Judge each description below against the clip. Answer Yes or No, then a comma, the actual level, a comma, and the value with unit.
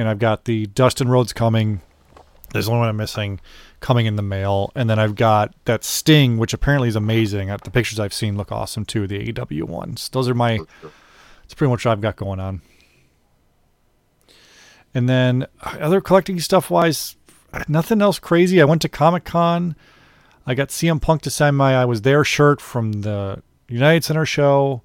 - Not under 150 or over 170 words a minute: No, average, 180 wpm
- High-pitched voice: No, low, 120 Hz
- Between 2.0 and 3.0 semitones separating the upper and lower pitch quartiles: No, wide, 5.6 semitones